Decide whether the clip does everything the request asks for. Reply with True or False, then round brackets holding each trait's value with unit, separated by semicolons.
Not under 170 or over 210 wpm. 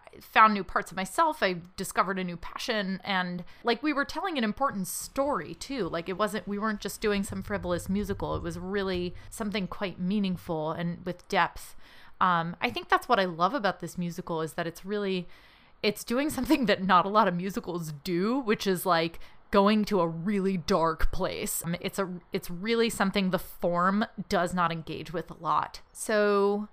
True (195 wpm)